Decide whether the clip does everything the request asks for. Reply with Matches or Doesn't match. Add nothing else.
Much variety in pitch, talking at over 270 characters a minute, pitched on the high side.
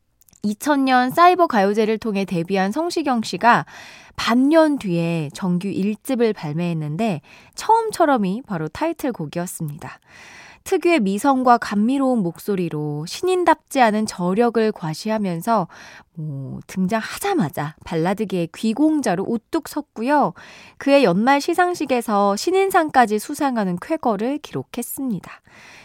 Matches